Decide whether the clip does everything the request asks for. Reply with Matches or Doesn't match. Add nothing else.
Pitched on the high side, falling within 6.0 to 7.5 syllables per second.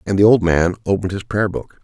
Doesn't match